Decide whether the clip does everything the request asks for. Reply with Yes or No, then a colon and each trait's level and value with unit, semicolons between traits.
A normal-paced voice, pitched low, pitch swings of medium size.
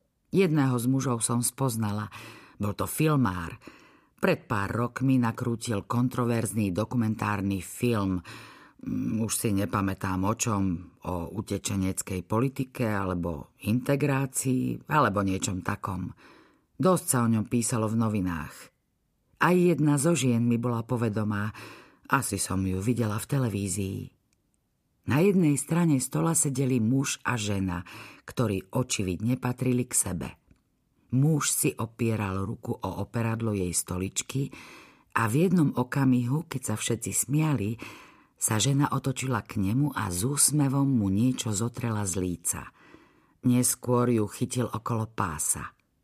Yes: average, 125 wpm; low, 115 Hz; average, 4.5 semitones